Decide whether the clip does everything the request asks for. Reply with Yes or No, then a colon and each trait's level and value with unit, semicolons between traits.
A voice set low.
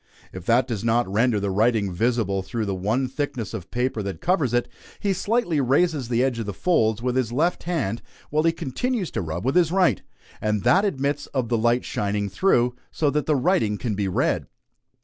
Yes: low, 120 Hz